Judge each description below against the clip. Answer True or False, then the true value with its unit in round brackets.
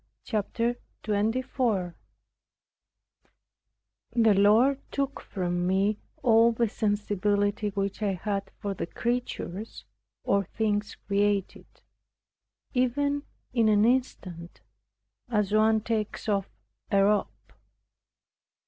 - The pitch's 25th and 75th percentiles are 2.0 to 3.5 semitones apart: True (2.6 semitones)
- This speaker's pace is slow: True (95 wpm)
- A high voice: True (210 Hz)